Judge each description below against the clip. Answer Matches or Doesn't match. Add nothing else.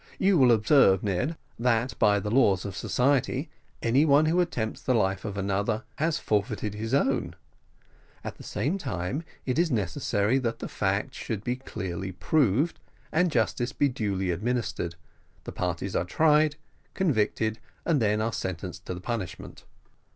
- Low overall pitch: Matches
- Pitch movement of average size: Doesn't match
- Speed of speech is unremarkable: Matches